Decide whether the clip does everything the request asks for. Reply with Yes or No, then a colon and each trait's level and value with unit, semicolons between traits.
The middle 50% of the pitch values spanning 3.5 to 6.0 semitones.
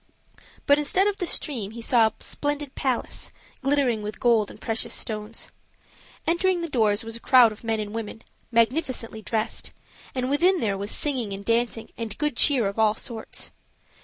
Yes: average, 4.5 semitones